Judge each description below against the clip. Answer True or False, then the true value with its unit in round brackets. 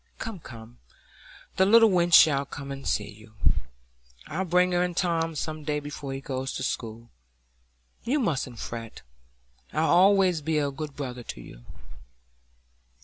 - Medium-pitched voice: True (150 Hz)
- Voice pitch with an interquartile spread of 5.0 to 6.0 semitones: True (5.6 semitones)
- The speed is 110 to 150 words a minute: True (145 wpm)